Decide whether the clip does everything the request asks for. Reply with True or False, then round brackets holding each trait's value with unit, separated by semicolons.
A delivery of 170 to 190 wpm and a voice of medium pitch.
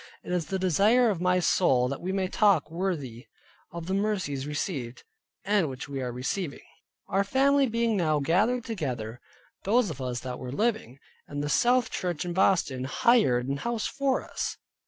True (175 wpm; 180 Hz)